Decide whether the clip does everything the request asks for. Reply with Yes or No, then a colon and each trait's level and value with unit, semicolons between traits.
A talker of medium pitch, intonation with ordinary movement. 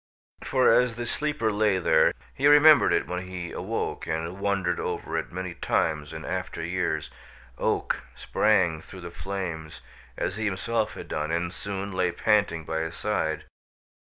No: very low, 95 Hz; average, 4.1 semitones